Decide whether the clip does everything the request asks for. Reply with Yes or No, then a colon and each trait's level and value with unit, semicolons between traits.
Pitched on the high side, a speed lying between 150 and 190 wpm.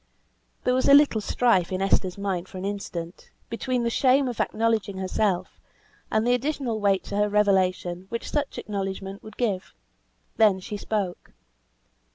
Yes: high, 205 Hz; average, 160 wpm